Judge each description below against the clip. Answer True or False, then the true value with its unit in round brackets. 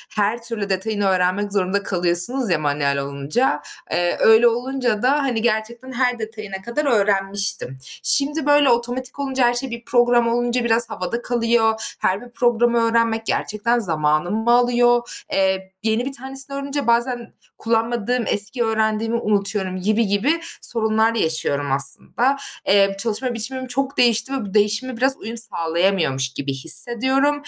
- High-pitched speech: True (230 Hz)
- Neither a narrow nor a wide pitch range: True (3.7 semitones)